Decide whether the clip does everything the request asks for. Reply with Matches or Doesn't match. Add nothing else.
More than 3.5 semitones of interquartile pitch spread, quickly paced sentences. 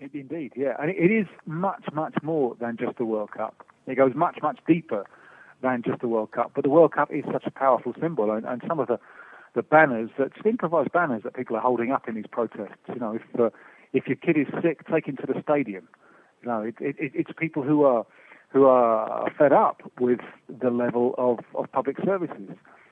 Matches